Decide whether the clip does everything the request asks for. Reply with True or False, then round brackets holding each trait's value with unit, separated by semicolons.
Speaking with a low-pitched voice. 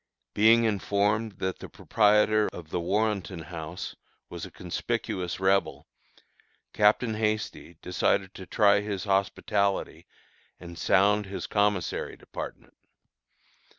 True (100 Hz)